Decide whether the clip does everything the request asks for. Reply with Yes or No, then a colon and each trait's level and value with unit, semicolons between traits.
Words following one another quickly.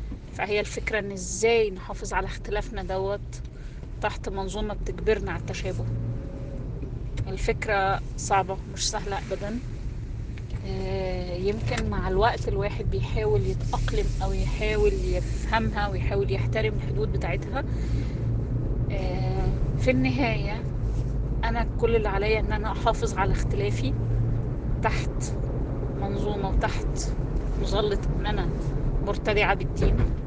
No: average, 100 wpm